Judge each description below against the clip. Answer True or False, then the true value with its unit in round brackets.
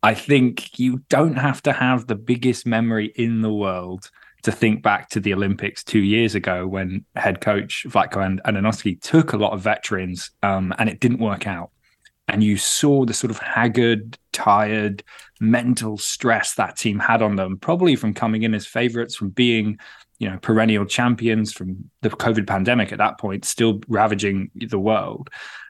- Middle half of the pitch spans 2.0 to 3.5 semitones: True (2.9 semitones)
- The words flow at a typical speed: True (175 wpm)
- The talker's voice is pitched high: False (110 Hz)